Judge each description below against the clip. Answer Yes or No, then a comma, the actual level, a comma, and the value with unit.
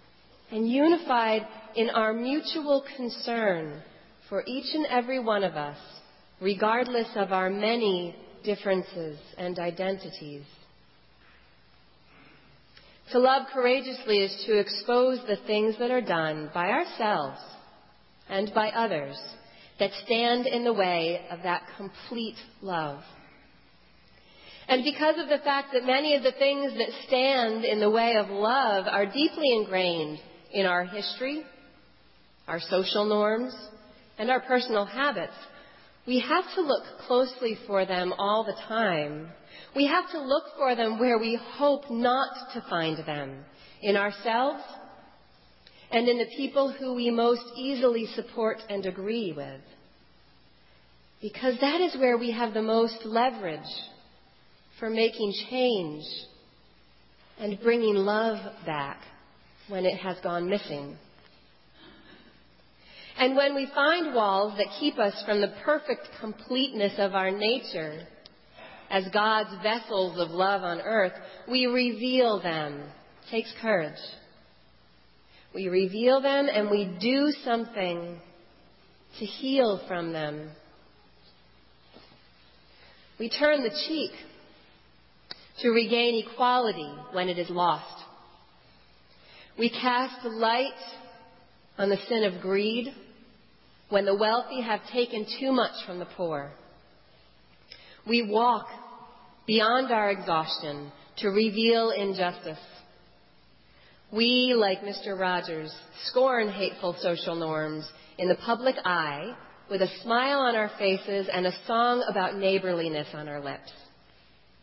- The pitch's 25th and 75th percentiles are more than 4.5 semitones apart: Yes, average, 5.1 semitones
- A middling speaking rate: No, slow, 125 wpm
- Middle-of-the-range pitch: No, high, 215 Hz